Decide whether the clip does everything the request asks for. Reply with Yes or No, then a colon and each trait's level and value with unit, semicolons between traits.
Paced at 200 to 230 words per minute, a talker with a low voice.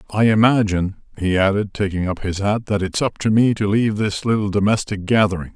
Yes: fast, 205 wpm; low, 100 Hz